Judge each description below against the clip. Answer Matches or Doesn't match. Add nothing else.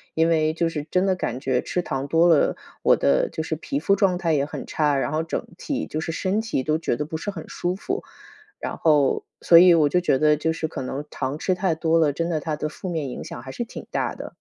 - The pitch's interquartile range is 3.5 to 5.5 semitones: Doesn't match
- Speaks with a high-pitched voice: Doesn't match